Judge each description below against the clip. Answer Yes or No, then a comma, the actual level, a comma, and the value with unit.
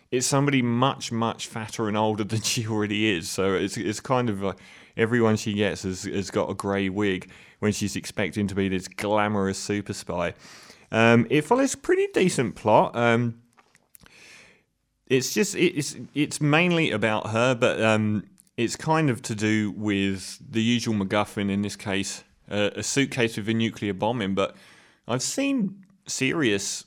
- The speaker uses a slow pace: No, average, 170 wpm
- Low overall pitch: Yes, low, 110 Hz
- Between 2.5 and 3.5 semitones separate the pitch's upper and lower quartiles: No, average, 3.9 semitones